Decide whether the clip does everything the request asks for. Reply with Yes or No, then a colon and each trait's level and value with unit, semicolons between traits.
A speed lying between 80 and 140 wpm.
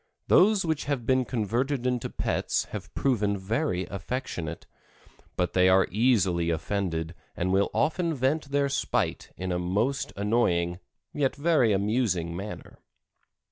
Yes: slow, 135 wpm